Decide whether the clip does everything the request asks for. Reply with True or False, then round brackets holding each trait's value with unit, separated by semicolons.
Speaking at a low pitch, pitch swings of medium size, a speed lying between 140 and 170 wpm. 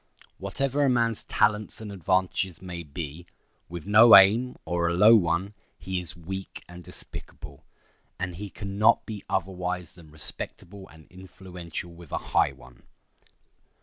True (95 Hz; 3.0 semitones; 150 wpm)